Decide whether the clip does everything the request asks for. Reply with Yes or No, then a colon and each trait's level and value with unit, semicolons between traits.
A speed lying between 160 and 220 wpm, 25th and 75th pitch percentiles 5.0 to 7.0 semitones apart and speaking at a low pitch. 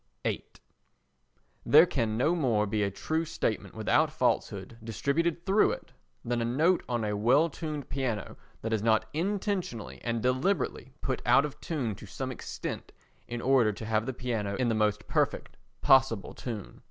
Yes: average, 165 wpm; average, 5.3 semitones; low, 125 Hz